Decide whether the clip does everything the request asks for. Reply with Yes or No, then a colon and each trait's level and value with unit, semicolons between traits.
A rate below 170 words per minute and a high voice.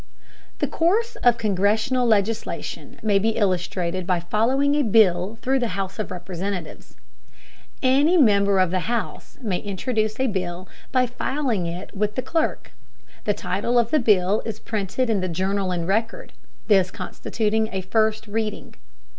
Yes: average, 155 wpm; high, 210 Hz